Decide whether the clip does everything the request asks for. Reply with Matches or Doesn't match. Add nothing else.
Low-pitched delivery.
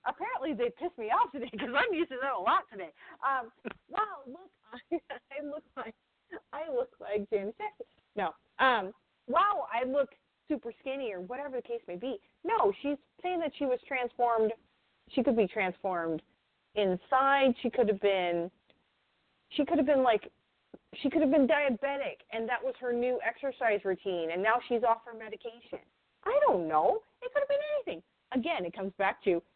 Doesn't match